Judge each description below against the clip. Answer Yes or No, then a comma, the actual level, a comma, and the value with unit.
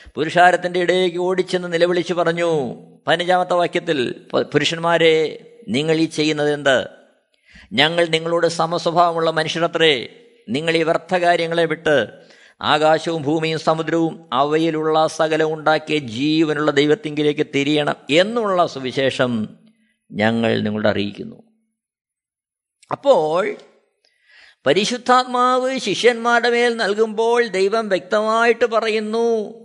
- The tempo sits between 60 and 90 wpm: Yes, average, 85 wpm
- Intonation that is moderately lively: No, wide, 5.8 semitones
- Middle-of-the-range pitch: Yes, medium, 170 Hz